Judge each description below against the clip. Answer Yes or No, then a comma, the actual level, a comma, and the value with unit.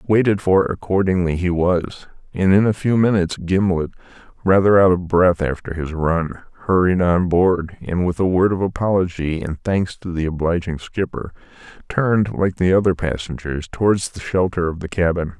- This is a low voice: Yes, very low, 90 Hz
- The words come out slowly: No, average, 170 wpm